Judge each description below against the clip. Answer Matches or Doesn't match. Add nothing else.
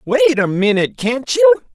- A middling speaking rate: Matches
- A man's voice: Matches